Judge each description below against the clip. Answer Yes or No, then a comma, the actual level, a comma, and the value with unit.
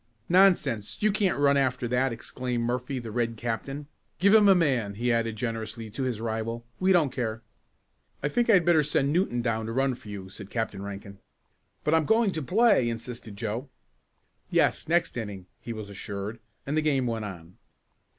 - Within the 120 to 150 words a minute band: No, average, 190 wpm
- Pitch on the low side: Yes, low, 120 Hz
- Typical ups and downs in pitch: Yes, average, 5.0 semitones